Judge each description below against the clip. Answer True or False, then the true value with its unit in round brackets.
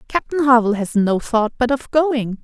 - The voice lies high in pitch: True (245 Hz)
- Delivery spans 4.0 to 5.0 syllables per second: True (4.9 syllables/s)